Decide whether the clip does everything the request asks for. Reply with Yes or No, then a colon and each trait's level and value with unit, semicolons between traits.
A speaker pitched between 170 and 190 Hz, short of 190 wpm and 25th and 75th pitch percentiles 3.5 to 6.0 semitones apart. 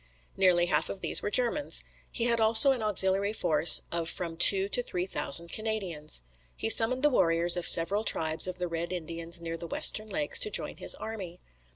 No: medium, 185 Hz; average, 195 wpm; average, 4.6 semitones